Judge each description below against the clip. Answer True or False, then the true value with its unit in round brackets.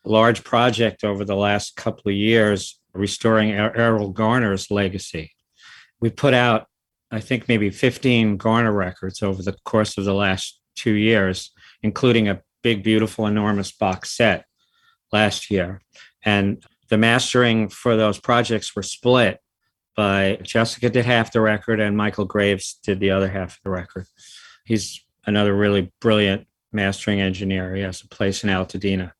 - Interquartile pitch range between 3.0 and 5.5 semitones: False (2.6 semitones)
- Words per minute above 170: False (155 wpm)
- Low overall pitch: True (105 Hz)